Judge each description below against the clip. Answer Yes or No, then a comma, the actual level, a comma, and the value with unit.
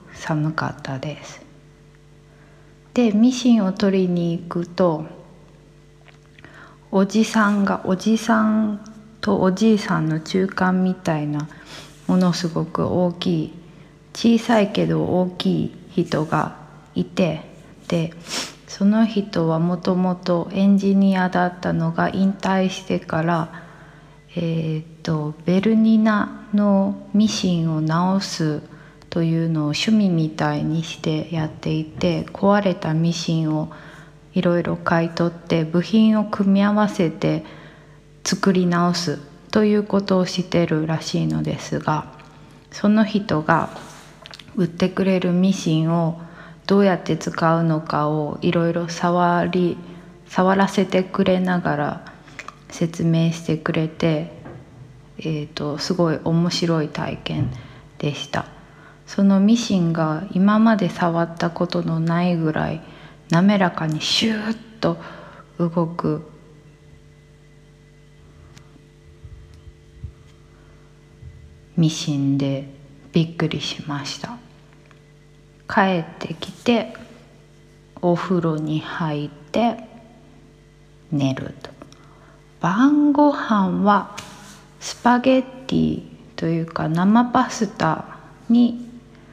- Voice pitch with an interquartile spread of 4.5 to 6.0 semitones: No, average, 4.0 semitones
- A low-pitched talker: No, medium, 170 Hz